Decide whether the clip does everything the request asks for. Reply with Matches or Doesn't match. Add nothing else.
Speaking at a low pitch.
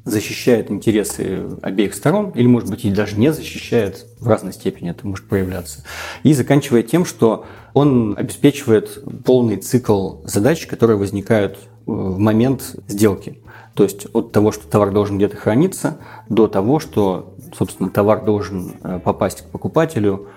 Matches